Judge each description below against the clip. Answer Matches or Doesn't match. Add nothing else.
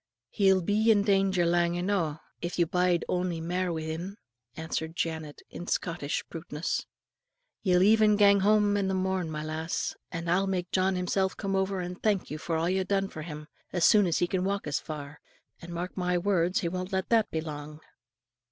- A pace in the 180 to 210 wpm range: Matches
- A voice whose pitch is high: Doesn't match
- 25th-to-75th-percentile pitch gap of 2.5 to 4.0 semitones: Matches